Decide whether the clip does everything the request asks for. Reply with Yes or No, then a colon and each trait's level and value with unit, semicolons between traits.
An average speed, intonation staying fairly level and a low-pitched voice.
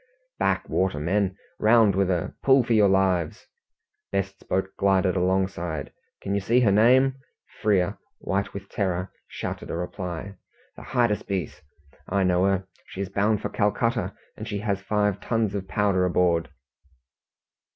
Yes: average, 150 wpm; narrow, 2.1 semitones; low, 100 Hz